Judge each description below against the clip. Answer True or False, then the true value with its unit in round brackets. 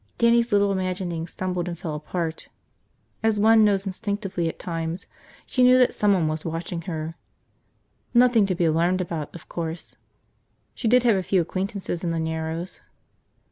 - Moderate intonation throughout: True (3.7 semitones)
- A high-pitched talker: False (180 Hz)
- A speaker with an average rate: True (160 wpm)